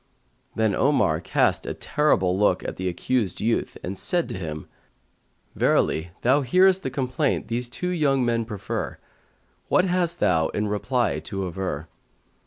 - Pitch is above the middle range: No, low, 115 Hz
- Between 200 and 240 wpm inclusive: No, average, 150 wpm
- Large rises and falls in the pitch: Yes, wide, 7.5 semitones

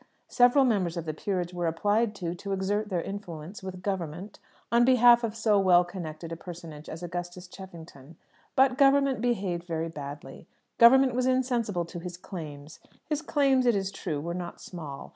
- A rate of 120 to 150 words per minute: No, average, 175 wpm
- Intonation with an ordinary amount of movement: No, wide, 5.7 semitones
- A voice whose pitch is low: No, medium, 185 Hz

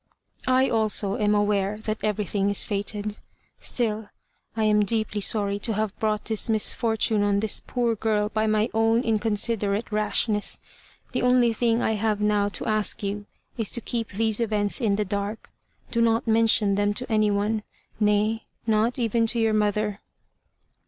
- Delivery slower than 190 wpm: Yes, average, 165 wpm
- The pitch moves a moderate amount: No, narrow, 1.4 semitones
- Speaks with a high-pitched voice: Yes, high, 215 Hz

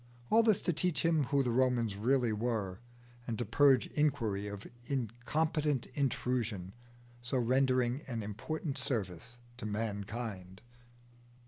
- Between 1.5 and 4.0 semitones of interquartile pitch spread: No, average, 4.5 semitones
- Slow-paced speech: Yes, slow, 125 wpm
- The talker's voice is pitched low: Yes, low, 120 Hz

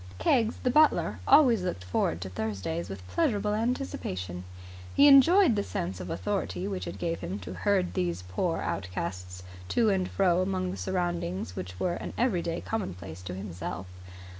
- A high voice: No, medium, 170 Hz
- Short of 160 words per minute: No, average, 165 wpm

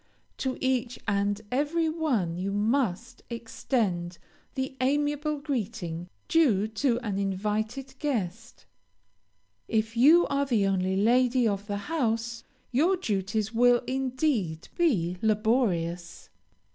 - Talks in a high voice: Yes, high, 230 Hz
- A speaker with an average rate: No, slow, 110 wpm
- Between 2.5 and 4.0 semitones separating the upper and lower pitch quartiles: No, average, 5.0 semitones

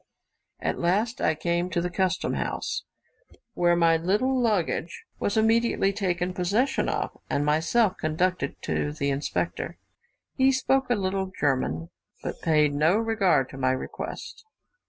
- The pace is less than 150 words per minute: Yes, average, 140 wpm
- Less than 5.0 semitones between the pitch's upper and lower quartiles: No, wide, 5.6 semitones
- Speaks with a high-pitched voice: No, medium, 180 Hz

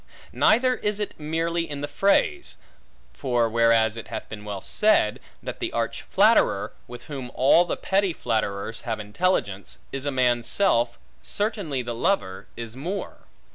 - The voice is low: Yes, low, 130 Hz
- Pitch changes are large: Yes, wide, 7.9 semitones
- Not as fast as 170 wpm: Yes, average, 155 wpm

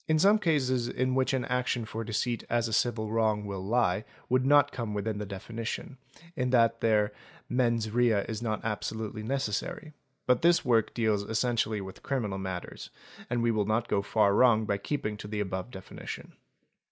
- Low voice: Yes, low, 115 Hz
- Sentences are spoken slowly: No, average, 175 wpm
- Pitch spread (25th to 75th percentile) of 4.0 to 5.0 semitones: No, average, 3.0 semitones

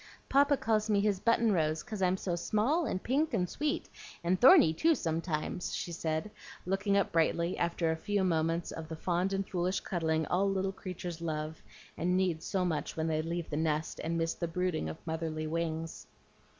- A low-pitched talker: No, medium, 175 Hz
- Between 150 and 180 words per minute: No, average, 190 wpm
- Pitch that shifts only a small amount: No, average, 3.3 semitones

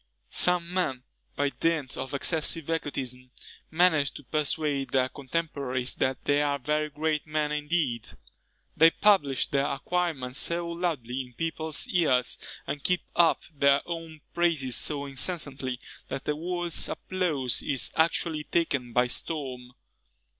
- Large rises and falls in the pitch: No, average, 3.7 semitones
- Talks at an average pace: No, slow, 130 wpm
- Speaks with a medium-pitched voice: Yes, medium, 150 Hz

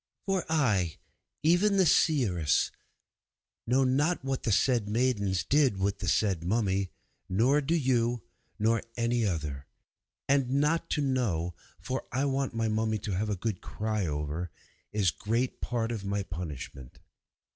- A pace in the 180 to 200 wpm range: No, average, 150 wpm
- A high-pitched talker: No, low, 115 Hz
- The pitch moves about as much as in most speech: No, wide, 5.7 semitones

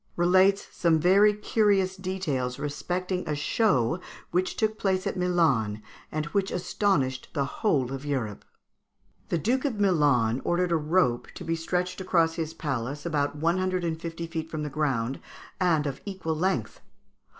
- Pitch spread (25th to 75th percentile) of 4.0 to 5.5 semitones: Yes, average, 4.3 semitones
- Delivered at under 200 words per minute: Yes, average, 160 wpm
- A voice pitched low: No, medium, 165 Hz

